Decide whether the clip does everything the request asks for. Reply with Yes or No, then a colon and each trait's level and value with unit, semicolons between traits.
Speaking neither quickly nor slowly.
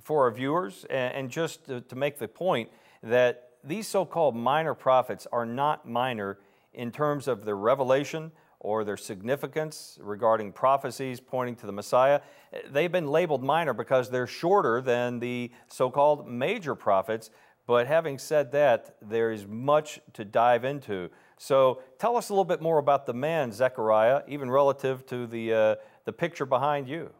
Yes: average, 165 wpm